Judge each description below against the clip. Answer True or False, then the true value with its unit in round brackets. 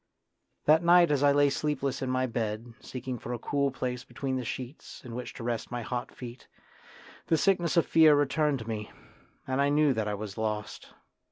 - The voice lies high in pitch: False (130 Hz)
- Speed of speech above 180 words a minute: True (200 wpm)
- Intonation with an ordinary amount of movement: True (3.6 semitones)